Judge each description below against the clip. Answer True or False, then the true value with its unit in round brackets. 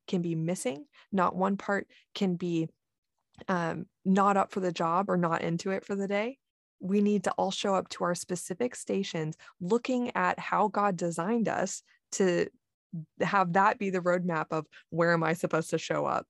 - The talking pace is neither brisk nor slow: True (190 wpm)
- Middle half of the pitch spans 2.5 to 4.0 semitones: True (2.9 semitones)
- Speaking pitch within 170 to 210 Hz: True (185 Hz)